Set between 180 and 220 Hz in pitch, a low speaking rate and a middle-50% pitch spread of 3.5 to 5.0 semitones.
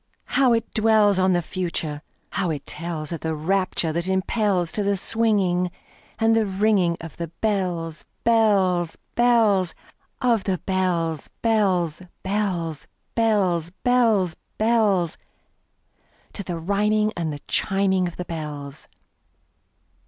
Yes: high, 190 Hz; slow, 110 wpm; average, 4.0 semitones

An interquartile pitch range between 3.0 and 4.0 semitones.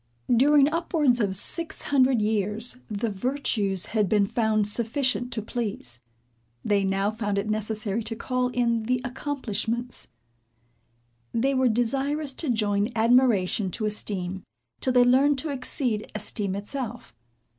Yes: average, 3.6 semitones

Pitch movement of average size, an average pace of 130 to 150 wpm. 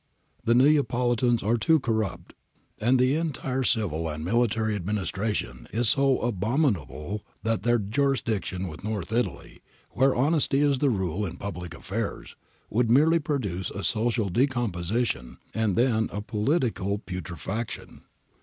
Yes: average, 4.6 semitones; slow, 135 wpm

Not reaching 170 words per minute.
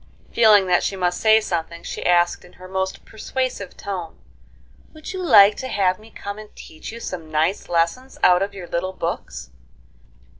No: average, 180 wpm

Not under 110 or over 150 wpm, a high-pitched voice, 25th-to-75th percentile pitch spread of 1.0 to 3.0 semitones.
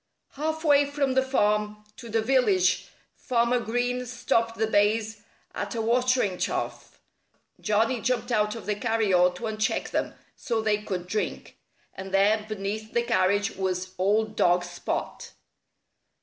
Yes: average, 145 wpm; high, 220 Hz; average, 2.7 semitones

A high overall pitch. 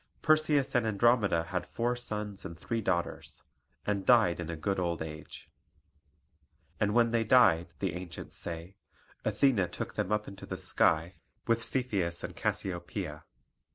No: low, 100 Hz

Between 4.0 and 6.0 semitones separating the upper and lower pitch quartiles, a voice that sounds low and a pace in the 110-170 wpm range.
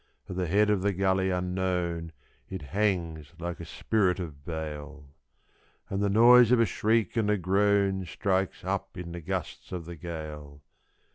No: average, 3.3 semitones; very low, 90 Hz; average, 165 wpm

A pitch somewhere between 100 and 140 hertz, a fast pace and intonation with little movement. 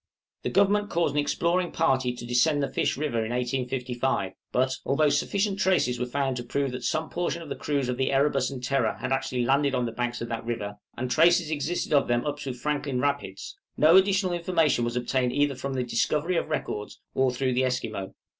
No: low, 135 Hz; fast, 210 wpm; average, 3.6 semitones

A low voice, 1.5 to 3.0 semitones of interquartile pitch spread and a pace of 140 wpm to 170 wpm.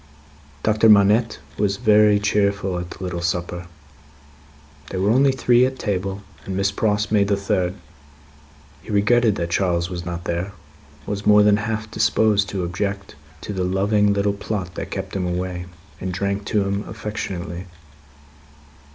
Yes: low, 100 Hz; narrow, 2.4 semitones; average, 155 wpm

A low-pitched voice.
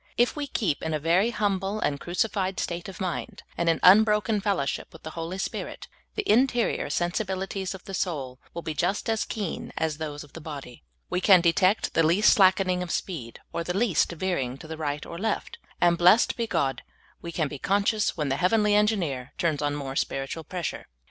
No: medium, 180 Hz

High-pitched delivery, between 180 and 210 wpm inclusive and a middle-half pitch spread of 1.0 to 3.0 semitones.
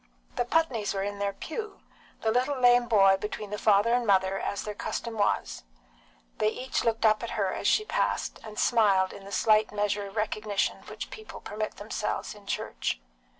Yes: high, 215 Hz; average, 190 wpm; narrow, 2.5 semitones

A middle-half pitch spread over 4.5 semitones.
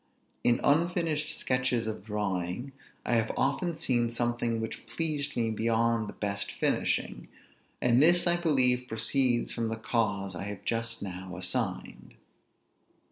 No: average, 4.0 semitones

